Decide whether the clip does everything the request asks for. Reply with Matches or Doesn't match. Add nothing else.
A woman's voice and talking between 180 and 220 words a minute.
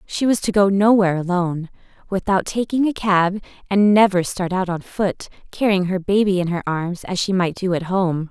Matches